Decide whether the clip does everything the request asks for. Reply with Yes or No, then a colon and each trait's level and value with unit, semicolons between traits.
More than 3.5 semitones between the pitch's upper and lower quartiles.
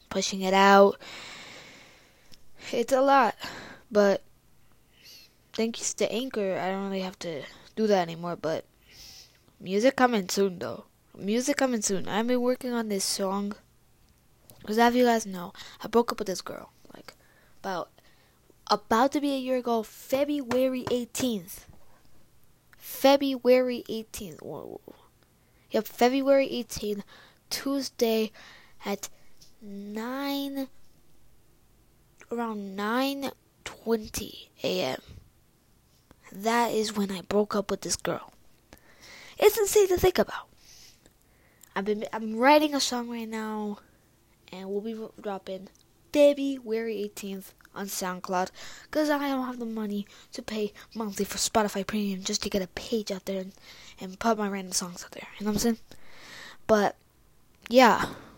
Yes: average, 4.2 semitones